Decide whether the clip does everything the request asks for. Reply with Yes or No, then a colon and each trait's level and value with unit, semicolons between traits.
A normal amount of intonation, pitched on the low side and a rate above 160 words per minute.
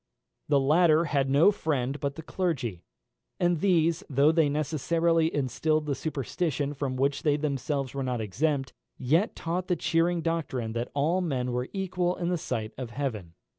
No: average, 3.9 semitones; medium, 150 Hz; average, 170 wpm